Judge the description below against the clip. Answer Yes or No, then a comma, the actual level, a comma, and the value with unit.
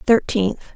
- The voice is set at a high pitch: Yes, high, 210 Hz